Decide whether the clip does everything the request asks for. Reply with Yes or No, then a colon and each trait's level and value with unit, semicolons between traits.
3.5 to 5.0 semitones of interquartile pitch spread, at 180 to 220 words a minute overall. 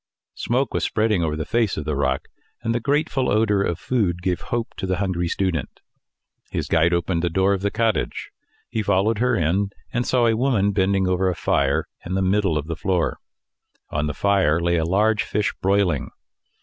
Yes: average, 4.0 semitones; average, 200 wpm